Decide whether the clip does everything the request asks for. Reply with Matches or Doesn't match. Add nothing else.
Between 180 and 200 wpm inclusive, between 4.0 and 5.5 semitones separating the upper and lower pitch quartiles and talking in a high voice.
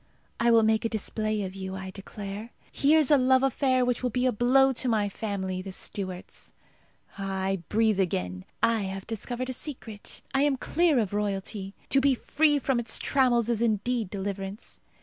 Matches